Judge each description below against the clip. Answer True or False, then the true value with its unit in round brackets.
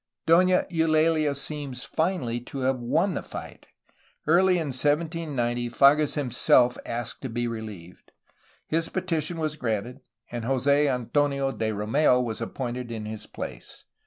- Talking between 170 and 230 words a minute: False (135 wpm)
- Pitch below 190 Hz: True (135 Hz)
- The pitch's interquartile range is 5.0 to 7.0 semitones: False (4.5 semitones)